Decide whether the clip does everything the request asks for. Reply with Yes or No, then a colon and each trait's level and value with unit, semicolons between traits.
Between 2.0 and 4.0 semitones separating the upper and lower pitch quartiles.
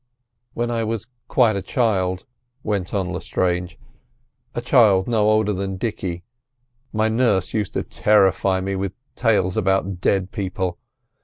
Yes: average, 2.7 semitones